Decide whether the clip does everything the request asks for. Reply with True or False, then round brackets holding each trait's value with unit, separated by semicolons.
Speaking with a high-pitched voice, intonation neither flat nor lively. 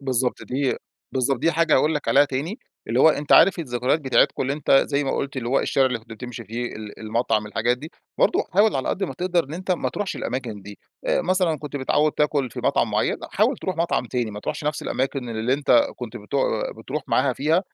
False (135 Hz; 4.3 semitones)